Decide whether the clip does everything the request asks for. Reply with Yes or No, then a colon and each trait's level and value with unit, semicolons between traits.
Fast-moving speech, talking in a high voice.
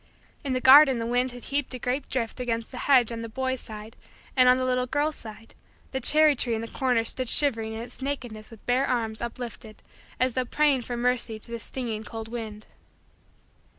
Yes: fast, 215 wpm; high, 245 Hz